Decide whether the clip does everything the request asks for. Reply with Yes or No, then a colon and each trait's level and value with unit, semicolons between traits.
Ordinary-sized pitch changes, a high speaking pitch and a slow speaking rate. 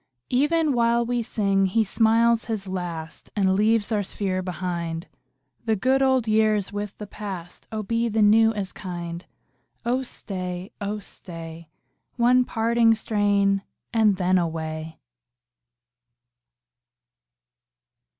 Yes: average, 3.7 semitones; high, 205 Hz; slow, 125 wpm